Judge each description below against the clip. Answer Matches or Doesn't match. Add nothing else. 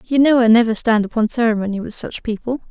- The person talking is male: Doesn't match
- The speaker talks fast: Matches